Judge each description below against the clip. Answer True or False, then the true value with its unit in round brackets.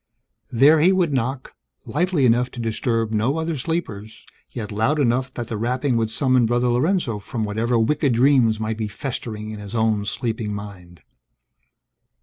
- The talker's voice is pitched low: True (120 Hz)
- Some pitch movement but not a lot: True (3.8 semitones)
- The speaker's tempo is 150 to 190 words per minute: True (160 wpm)